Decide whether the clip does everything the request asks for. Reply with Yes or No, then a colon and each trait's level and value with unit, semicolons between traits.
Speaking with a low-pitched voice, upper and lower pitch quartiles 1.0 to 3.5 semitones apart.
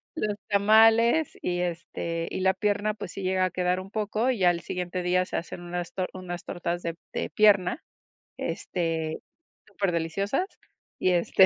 No: medium, 185 Hz; average, 2.7 semitones